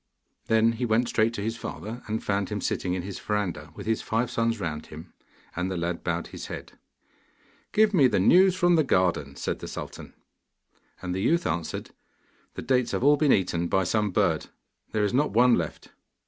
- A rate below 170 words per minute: No, average, 200 wpm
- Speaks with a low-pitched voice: Yes, low, 105 Hz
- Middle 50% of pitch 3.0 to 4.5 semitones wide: No, wide, 5.4 semitones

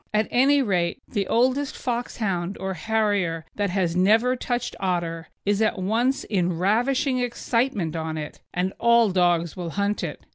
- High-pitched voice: Yes, high, 205 Hz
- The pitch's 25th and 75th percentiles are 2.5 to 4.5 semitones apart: No, average, 5.1 semitones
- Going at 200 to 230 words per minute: No, average, 155 wpm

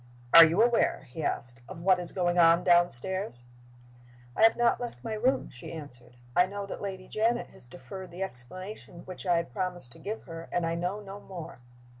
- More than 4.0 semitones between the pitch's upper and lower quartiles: No, average, 3.3 semitones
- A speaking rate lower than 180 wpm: No, average, 200 wpm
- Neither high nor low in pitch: Yes, medium, 180 Hz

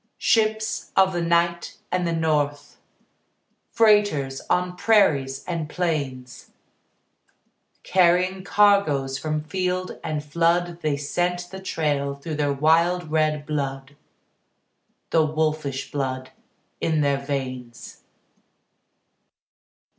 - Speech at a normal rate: No, slow, 100 wpm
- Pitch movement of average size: Yes, average, 3.9 semitones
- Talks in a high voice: No, medium, 155 Hz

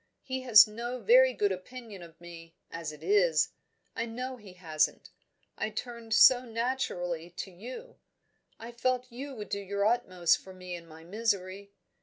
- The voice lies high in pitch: Yes, high, 210 Hz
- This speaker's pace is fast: No, average, 165 wpm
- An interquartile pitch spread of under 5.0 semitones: No, average, 5.3 semitones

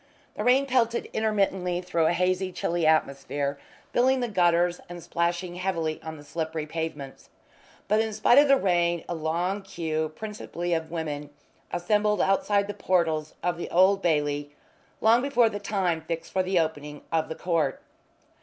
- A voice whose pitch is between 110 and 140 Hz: No, medium, 175 Hz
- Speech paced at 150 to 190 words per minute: Yes, average, 165 wpm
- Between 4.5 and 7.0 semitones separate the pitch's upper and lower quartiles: No, average, 4.0 semitones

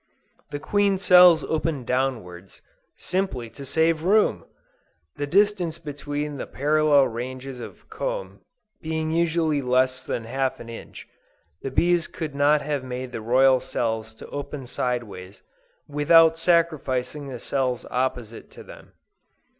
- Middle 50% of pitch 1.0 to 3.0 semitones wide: No, average, 4.2 semitones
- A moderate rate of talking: No, slow, 130 wpm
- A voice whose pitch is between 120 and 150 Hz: Yes, medium, 140 Hz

